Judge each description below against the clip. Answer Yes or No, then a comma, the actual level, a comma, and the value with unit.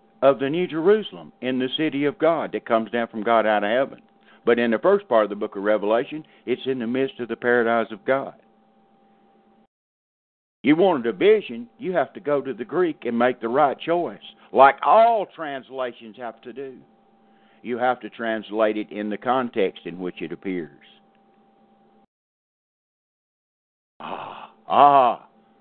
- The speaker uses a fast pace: No, average, 170 wpm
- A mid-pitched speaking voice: No, low, 130 Hz